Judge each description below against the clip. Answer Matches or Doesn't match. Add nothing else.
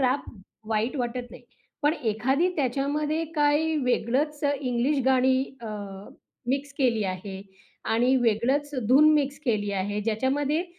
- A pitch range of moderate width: Matches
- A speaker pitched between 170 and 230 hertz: Doesn't match